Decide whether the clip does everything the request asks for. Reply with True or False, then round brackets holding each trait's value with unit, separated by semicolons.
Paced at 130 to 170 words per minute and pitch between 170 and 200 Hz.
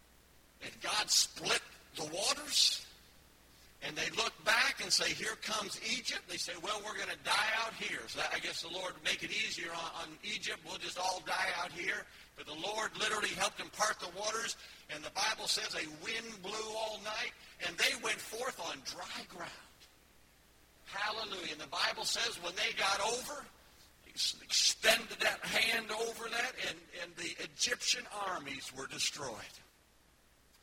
True (165 wpm; 185 Hz)